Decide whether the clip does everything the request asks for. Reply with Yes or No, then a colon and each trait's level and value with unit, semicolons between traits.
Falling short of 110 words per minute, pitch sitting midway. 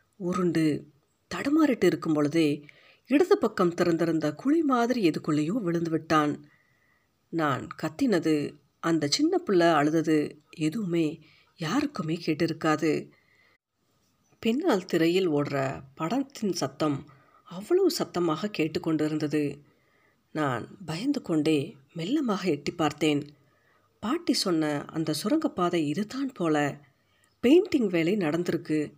Yes: average, 90 wpm; medium, 165 Hz